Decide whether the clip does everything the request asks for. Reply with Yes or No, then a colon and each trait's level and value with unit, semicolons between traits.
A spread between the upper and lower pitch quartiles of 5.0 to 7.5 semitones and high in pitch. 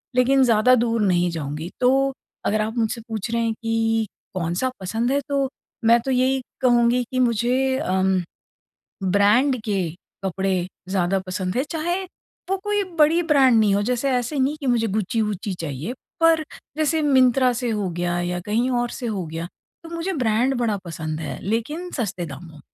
Yes: average, 5.3 semitones; high, 230 Hz